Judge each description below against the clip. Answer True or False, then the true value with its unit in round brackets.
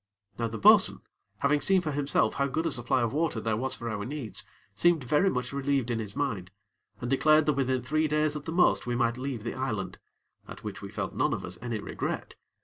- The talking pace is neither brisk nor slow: False (230 wpm)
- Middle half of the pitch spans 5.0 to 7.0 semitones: False (4.2 semitones)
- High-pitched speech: False (130 Hz)